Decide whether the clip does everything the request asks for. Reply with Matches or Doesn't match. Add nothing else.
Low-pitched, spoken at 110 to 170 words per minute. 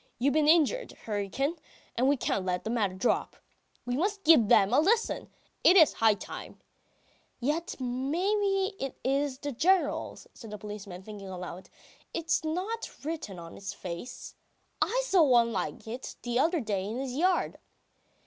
Doesn't match